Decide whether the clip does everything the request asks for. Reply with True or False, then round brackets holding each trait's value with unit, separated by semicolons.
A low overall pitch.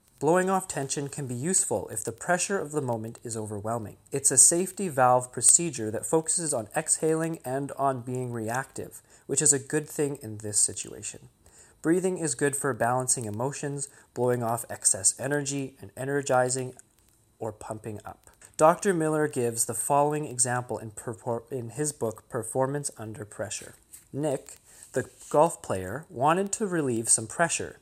True (130 Hz)